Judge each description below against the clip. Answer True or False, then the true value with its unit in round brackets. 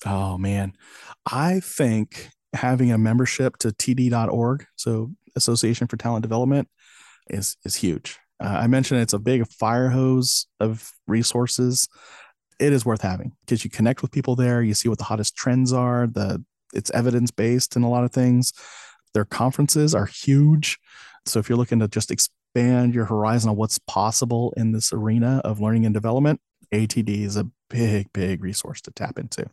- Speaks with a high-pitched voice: False (120 Hz)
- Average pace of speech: True (175 wpm)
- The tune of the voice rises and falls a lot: False (2.5 semitones)